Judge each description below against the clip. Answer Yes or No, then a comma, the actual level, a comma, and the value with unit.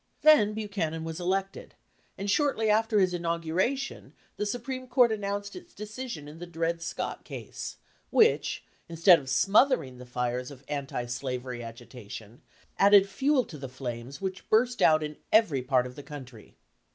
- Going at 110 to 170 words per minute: Yes, average, 160 wpm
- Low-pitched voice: No, medium, 170 Hz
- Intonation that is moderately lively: No, wide, 8.3 semitones